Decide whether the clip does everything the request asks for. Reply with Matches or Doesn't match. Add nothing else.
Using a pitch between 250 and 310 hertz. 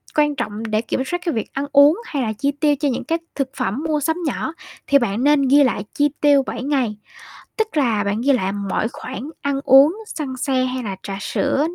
Matches